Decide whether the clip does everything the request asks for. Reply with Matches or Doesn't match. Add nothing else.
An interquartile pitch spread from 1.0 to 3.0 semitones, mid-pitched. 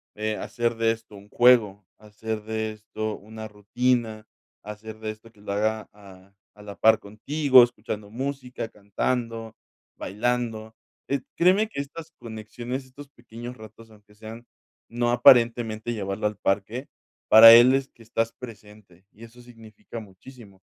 Doesn't match